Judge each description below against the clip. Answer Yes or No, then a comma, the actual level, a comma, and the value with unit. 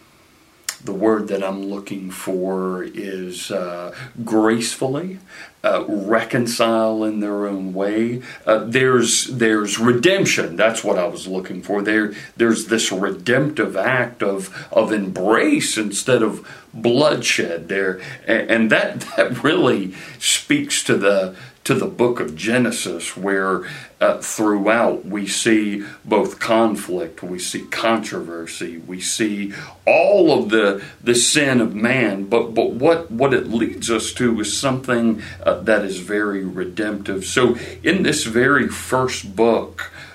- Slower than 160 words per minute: Yes, slow, 135 wpm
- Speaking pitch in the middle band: No, low, 110 Hz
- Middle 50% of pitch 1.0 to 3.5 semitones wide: Yes, average, 3.1 semitones